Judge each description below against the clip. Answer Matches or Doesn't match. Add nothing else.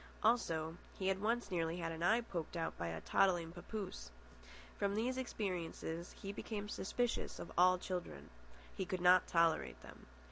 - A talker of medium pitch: Matches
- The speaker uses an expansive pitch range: Doesn't match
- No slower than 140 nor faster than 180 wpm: Matches